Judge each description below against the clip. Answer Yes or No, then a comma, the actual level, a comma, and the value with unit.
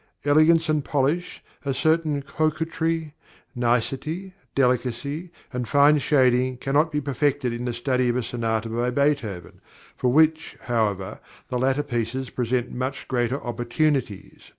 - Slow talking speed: Yes, slow, 130 wpm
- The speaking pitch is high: No, low, 130 Hz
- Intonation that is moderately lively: Yes, average, 3.6 semitones